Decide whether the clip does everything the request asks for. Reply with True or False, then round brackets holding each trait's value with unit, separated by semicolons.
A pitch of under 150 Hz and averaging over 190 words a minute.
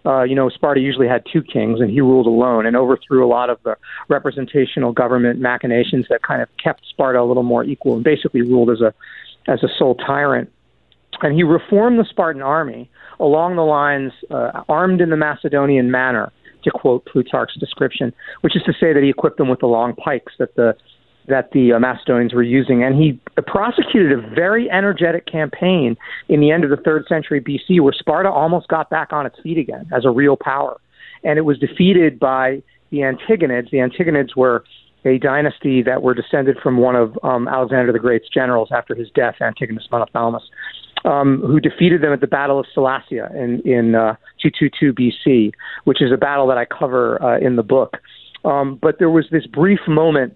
True (135 Hz; 200 wpm)